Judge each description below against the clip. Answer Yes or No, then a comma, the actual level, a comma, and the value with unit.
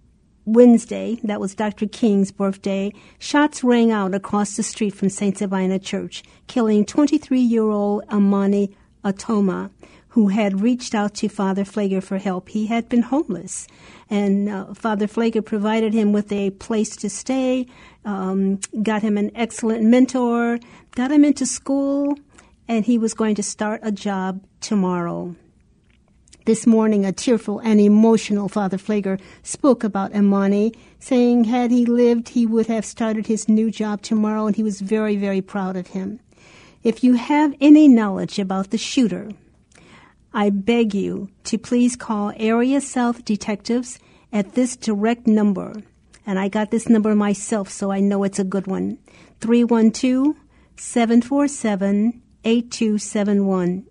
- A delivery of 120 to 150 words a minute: Yes, average, 145 wpm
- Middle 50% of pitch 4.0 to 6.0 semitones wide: No, average, 2.8 semitones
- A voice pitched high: Yes, high, 215 Hz